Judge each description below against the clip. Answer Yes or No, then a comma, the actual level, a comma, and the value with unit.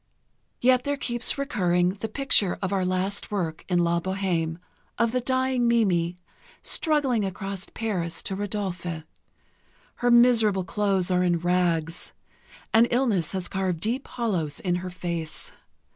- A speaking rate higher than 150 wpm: No, average, 140 wpm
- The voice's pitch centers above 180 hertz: Yes, high, 190 Hz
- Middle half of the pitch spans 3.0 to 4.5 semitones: No, average, 4.9 semitones